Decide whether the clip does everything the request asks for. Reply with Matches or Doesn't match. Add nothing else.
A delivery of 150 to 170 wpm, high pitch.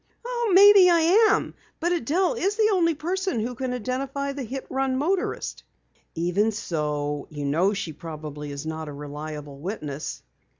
Matches